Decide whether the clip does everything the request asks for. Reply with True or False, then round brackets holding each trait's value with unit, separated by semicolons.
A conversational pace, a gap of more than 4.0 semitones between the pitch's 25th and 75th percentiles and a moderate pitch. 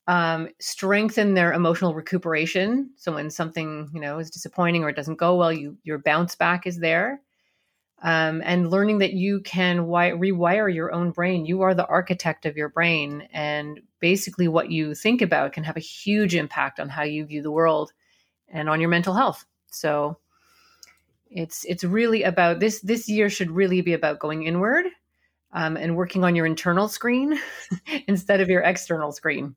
False (180 wpm; 3.4 semitones; 175 Hz)